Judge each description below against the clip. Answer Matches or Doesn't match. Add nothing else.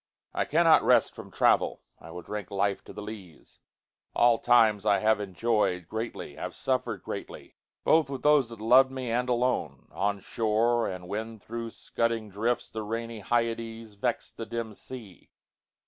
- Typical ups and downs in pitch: Doesn't match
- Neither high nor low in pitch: Doesn't match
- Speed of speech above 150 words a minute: Doesn't match